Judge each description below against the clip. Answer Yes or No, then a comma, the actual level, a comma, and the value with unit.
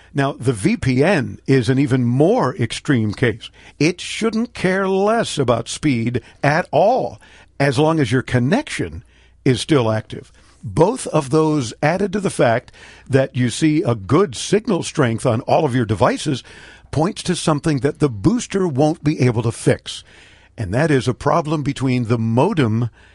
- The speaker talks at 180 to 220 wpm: No, average, 165 wpm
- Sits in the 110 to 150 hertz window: Yes, low, 135 Hz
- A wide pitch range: No, average, 4.5 semitones